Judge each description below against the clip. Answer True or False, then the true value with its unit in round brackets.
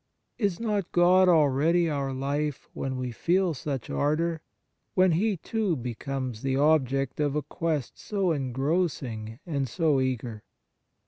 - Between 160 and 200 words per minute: False (135 wpm)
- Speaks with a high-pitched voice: False (150 Hz)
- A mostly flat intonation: False (4.6 semitones)